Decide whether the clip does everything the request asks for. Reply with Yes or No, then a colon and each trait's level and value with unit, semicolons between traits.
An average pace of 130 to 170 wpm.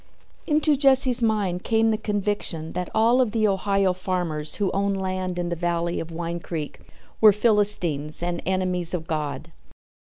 Yes: average, 160 wpm